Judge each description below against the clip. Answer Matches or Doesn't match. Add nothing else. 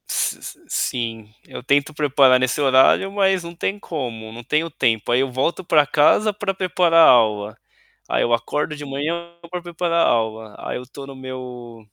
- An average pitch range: Doesn't match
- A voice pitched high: Doesn't match